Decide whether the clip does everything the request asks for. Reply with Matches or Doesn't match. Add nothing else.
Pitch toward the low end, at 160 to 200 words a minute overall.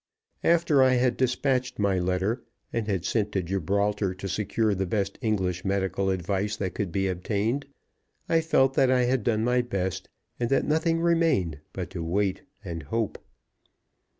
Matches